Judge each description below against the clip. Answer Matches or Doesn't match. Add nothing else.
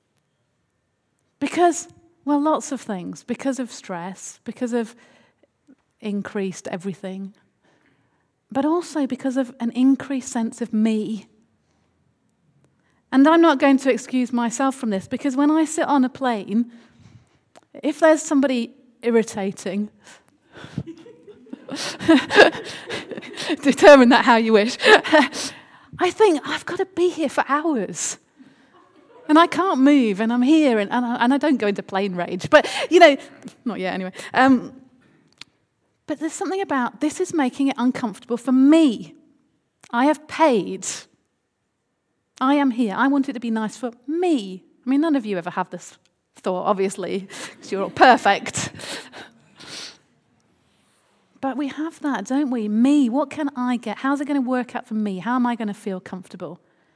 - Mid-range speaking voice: Doesn't match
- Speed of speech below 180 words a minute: Matches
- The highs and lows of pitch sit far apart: Doesn't match